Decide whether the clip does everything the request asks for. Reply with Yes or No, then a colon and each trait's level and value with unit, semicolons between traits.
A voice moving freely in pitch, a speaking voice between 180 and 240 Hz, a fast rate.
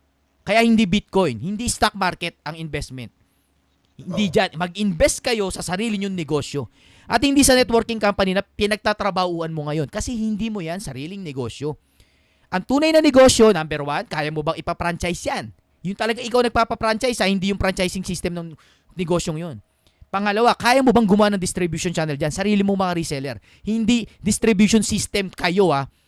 Yes: wide, 5.9 semitones; medium, 185 Hz; fast, 165 wpm